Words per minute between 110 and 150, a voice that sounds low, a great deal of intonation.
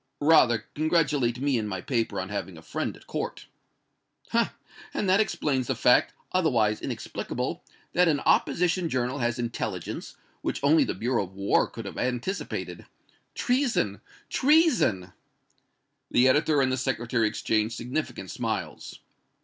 Yes: average, 140 wpm; low, 125 Hz; wide, 5.8 semitones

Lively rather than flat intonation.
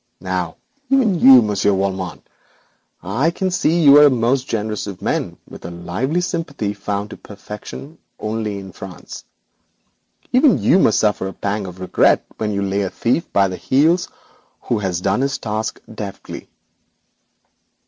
Yes: wide, 6.1 semitones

